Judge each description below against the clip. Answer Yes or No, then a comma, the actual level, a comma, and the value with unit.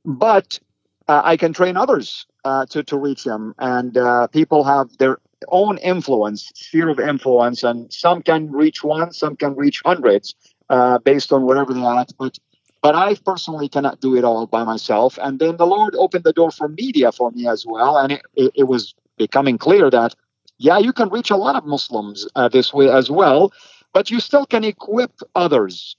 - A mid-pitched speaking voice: Yes, medium, 145 Hz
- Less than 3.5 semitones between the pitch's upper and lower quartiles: No, average, 5.2 semitones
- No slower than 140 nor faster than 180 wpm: No, average, 195 wpm